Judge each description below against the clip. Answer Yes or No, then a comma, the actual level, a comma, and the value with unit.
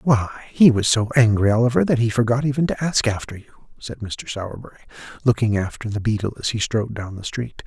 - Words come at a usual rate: No, fast, 210 wpm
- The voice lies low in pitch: Yes, low, 115 Hz